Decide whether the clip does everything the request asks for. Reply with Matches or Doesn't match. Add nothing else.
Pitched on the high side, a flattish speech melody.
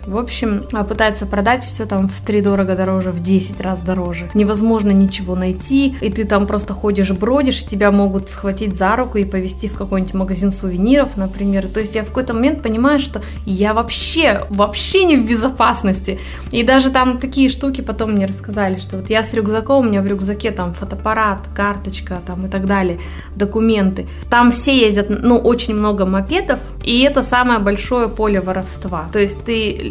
Doesn't match